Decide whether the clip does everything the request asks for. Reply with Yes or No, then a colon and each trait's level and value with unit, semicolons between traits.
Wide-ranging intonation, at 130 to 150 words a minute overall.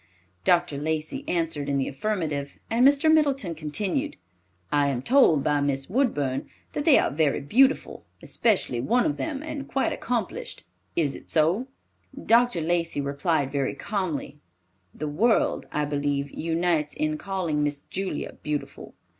Yes: wide, 8.1 semitones; average, 145 wpm